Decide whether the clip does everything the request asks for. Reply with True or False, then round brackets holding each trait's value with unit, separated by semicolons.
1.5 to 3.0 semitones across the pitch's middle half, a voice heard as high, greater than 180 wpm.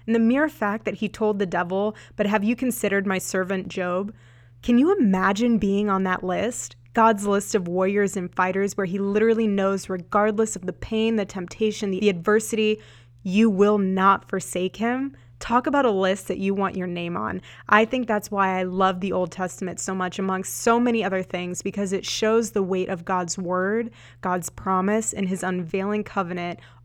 True (2.6 semitones; 195 Hz; 190 wpm)